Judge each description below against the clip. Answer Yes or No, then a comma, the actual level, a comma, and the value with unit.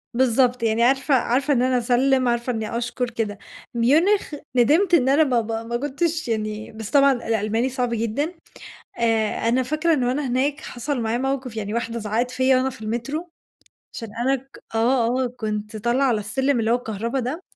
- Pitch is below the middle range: No, high, 245 Hz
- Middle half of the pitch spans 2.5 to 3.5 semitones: Yes, average, 2.8 semitones